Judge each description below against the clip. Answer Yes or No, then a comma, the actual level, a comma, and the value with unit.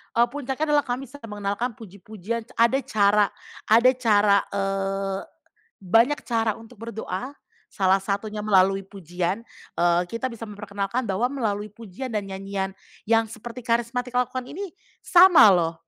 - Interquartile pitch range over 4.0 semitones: No, average, 3.7 semitones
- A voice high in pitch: Yes, high, 215 Hz